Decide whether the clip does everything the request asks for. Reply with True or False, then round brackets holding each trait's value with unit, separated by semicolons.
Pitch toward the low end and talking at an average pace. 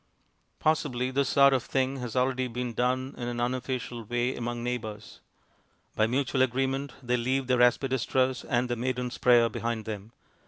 True (125 Hz; 160 wpm)